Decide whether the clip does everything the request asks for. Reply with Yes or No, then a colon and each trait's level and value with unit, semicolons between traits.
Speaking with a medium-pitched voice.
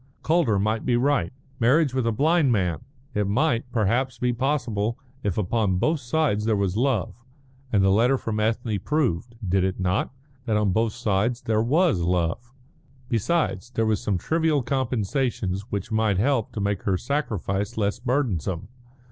No: low, 110 Hz